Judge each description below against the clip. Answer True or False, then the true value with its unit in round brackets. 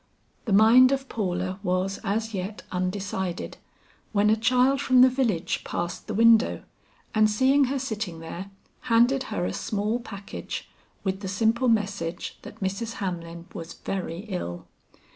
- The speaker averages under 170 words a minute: True (145 wpm)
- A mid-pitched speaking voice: False (210 Hz)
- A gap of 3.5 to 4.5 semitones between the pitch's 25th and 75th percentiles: True (3.8 semitones)